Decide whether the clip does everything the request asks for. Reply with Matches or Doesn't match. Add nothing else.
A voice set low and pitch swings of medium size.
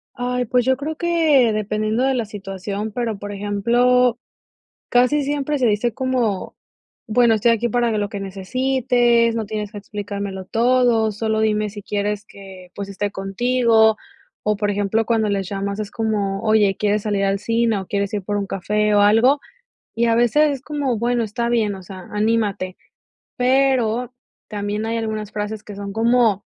Doesn't match